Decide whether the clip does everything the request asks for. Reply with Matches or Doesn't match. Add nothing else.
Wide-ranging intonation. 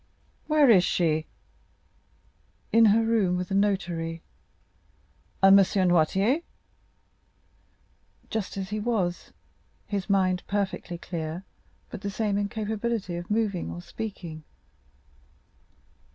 Doesn't match